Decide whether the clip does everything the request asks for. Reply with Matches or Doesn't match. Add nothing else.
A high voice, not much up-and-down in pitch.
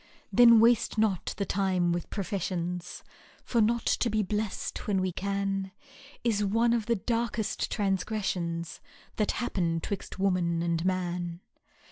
Doesn't match